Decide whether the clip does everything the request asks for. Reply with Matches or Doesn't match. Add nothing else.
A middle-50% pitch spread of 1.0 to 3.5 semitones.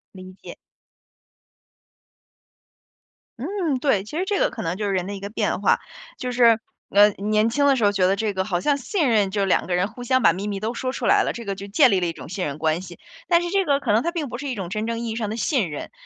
Doesn't match